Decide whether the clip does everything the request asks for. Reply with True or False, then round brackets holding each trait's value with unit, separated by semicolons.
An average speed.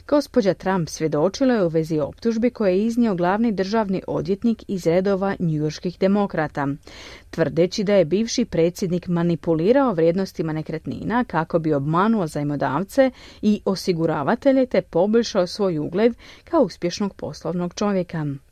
True (125 wpm)